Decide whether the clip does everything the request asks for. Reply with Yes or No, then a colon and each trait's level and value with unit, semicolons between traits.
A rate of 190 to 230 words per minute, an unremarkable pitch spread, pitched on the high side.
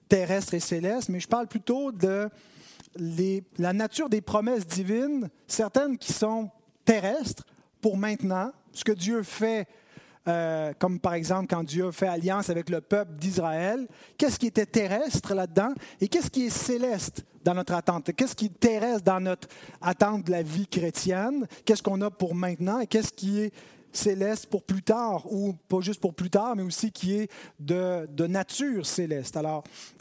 No: average, 175 wpm; average, 3.5 semitones; high, 195 Hz